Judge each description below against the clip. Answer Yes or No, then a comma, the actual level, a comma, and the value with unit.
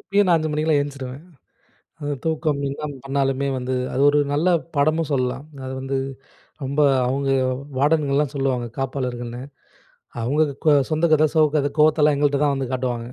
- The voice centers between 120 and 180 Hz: Yes, medium, 140 Hz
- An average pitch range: No, narrow, 2.3 semitones